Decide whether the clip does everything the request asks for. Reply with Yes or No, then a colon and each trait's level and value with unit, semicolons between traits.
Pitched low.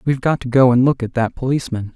Yes: low, 125 Hz